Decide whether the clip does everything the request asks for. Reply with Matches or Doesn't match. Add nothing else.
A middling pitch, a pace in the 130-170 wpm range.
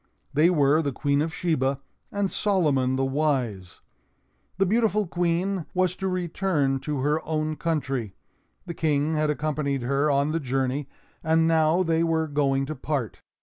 Matches